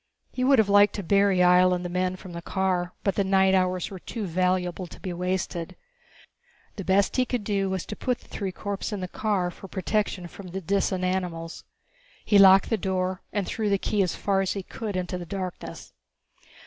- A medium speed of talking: No, fast, 210 wpm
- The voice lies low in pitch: No, high, 190 Hz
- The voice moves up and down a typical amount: No, narrow, 1.7 semitones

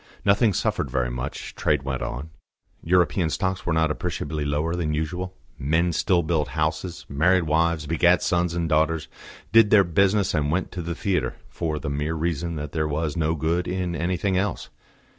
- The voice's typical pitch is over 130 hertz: No, very low, 80 Hz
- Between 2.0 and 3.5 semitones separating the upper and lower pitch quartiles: Yes, narrow, 2.6 semitones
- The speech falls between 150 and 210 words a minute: Yes, average, 180 wpm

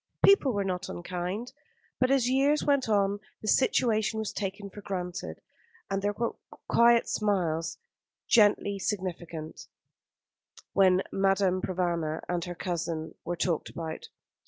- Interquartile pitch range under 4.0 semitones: Yes, average, 3.5 semitones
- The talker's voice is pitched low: No, high, 195 Hz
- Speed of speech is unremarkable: No, slow, 130 wpm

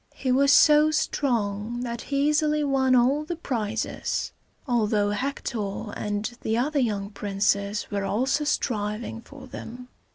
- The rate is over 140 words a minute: No, slow, 135 wpm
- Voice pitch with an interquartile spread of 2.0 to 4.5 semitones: No, average, 5.1 semitones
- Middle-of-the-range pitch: No, high, 240 Hz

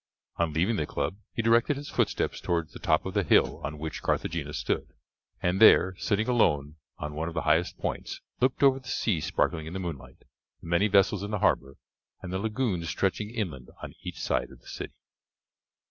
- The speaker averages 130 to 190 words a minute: No, average, 200 wpm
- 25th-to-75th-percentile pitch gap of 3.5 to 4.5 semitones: No, wide, 5.4 semitones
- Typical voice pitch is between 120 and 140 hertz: No, very low, 90 Hz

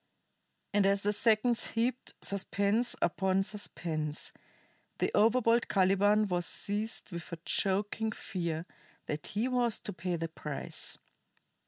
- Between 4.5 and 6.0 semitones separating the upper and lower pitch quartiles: No, average, 3.7 semitones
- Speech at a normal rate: No, slow, 125 wpm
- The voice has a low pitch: No, high, 200 Hz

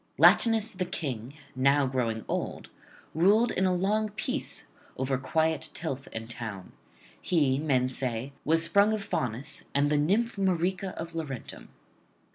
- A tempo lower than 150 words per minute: Yes, average, 140 wpm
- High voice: No, medium, 160 Hz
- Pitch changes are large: Yes, wide, 6.6 semitones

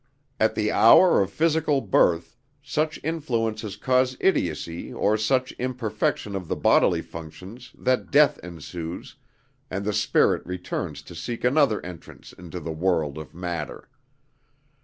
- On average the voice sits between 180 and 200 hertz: No, low, 105 Hz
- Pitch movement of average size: No, wide, 6.7 semitones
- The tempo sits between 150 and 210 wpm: No, slow, 135 wpm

